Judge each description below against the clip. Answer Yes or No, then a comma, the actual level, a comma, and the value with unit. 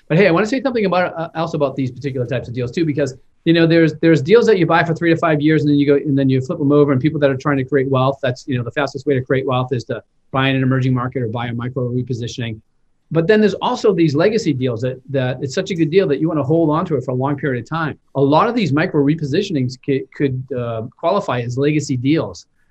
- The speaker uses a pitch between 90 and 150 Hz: Yes, medium, 140 Hz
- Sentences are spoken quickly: Yes, fast, 295 wpm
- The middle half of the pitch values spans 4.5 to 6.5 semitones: No, average, 3.8 semitones